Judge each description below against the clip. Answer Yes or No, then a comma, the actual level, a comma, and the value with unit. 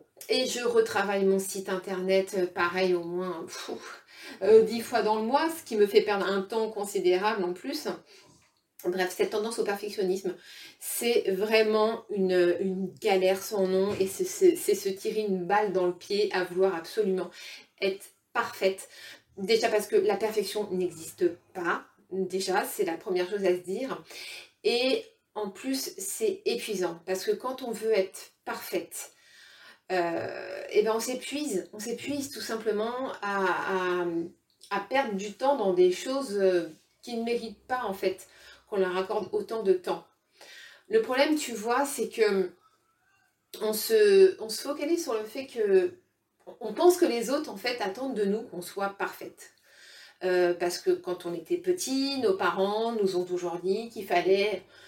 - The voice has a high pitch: Yes, high, 210 Hz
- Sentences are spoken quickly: No, average, 170 wpm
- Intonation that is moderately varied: No, wide, 5.9 semitones